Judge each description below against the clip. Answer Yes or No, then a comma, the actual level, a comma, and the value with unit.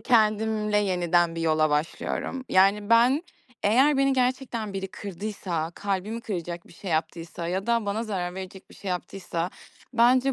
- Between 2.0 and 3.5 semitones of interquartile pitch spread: No, average, 4.7 semitones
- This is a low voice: No, high, 200 Hz